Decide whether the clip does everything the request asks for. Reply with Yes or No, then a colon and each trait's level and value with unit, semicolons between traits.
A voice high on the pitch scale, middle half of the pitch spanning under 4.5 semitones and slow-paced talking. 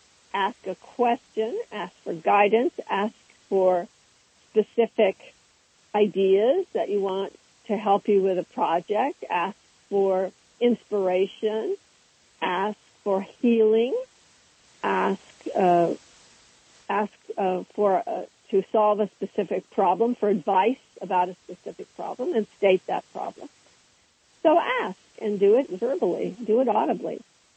Yes: high, 205 Hz; average, 3.3 semitones; slow, 120 wpm